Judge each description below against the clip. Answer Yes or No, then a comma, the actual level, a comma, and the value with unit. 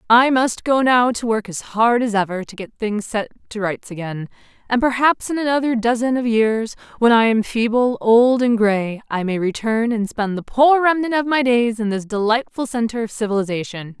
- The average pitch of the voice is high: Yes, high, 230 Hz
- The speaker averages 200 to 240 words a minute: Yes, fast, 205 wpm